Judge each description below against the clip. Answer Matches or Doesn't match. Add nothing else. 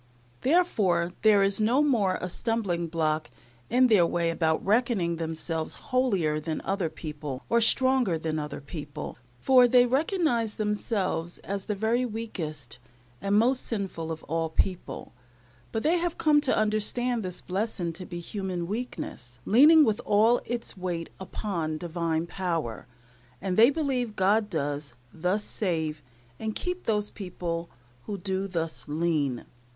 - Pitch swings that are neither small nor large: Doesn't match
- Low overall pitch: Doesn't match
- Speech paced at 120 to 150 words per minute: Matches